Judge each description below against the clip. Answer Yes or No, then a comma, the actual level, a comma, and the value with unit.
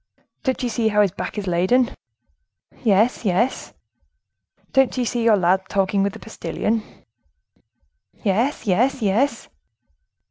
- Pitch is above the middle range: Yes, high, 220 Hz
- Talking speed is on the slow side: Yes, slow, 130 wpm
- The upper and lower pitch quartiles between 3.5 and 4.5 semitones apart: Yes, average, 4.1 semitones